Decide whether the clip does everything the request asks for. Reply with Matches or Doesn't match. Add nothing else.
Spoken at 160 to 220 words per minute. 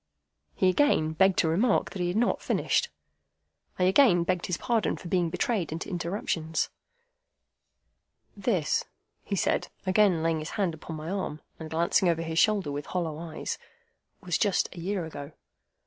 Matches